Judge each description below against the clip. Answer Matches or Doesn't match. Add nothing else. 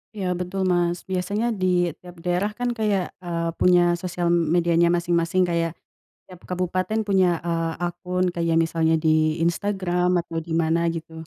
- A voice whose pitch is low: Doesn't match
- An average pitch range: Doesn't match